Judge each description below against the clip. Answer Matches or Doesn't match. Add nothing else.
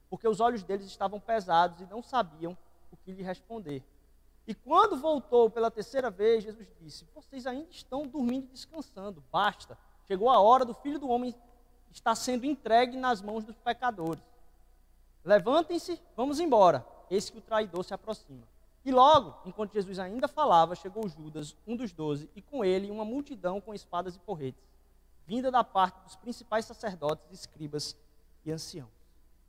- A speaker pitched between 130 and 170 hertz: Doesn't match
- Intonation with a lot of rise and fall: Matches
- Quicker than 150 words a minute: Matches